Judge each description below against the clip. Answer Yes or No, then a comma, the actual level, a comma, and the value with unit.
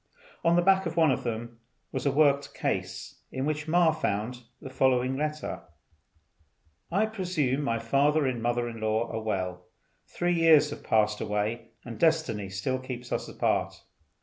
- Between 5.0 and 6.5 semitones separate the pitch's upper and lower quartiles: Yes, average, 5.3 semitones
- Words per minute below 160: No, average, 165 wpm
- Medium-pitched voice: No, low, 130 Hz